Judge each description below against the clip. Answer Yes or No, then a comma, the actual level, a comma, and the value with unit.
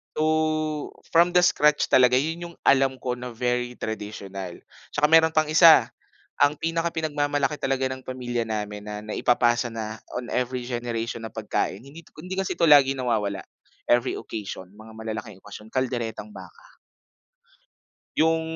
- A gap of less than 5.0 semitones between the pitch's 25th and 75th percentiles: No, wide, 5.6 semitones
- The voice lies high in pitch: No, low, 125 Hz